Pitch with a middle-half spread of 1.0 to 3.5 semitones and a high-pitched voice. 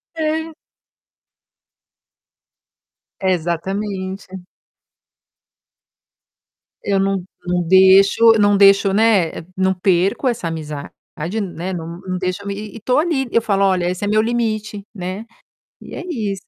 Yes: average, 2.8 semitones; high, 195 Hz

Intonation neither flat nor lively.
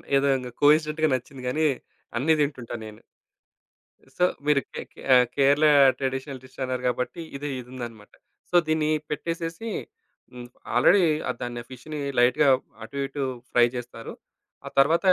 Yes: average, 3.6 semitones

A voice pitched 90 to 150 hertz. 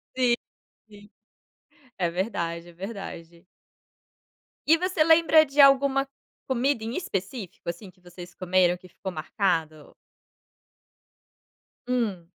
No: high, 195 Hz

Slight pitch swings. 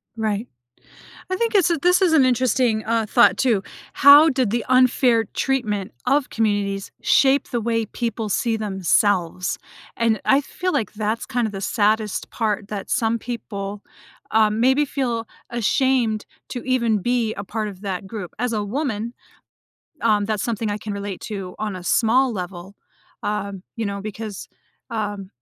No: average, 3.3 semitones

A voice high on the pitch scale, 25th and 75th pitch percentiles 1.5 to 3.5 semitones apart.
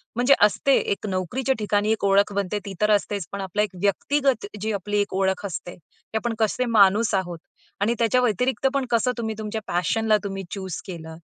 Yes: high, 210 Hz; average, 2.8 semitones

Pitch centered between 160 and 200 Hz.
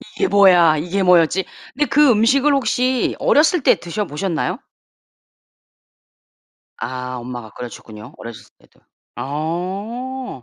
Yes: medium, 185 Hz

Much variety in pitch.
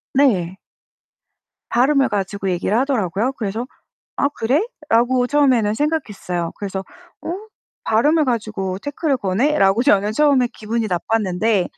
Yes: wide, 5.9 semitones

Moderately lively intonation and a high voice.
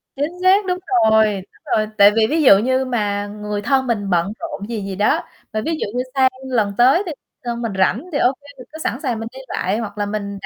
Yes: average, 4.3 semitones; high, 225 Hz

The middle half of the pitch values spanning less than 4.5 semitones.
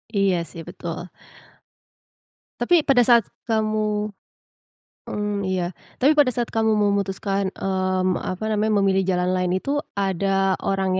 Yes: narrow, 2.4 semitones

